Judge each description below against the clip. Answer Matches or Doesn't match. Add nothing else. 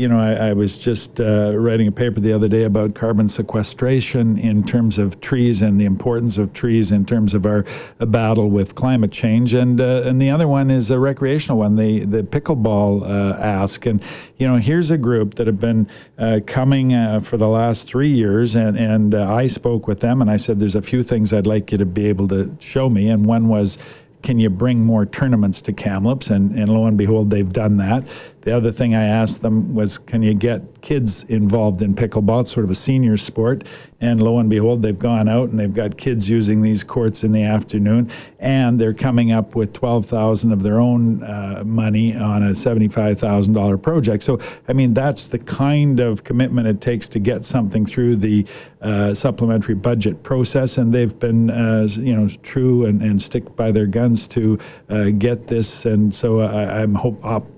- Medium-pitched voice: Doesn't match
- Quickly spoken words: Matches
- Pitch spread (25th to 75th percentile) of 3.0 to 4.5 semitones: Doesn't match